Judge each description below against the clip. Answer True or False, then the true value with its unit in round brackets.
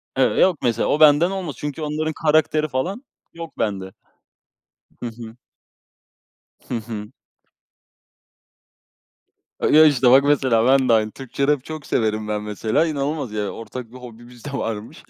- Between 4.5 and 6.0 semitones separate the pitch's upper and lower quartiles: True (5.1 semitones)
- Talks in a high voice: False (130 Hz)